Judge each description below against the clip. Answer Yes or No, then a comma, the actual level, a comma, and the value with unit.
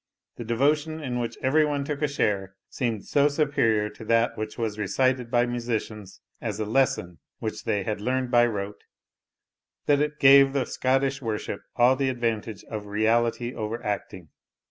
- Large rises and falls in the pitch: No, average, 3.9 semitones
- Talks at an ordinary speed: Yes, average, 165 wpm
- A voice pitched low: Yes, low, 120 Hz